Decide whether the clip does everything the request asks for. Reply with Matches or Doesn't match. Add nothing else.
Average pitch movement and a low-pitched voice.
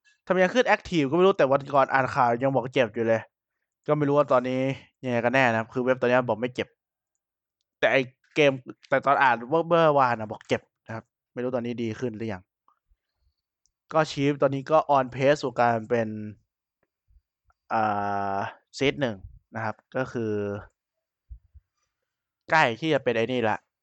Matches